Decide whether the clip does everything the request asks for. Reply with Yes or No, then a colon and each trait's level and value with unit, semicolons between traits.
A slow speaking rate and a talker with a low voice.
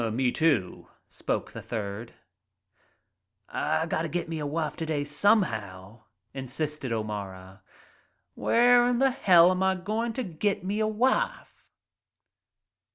No: slow, 125 wpm; medium, 155 Hz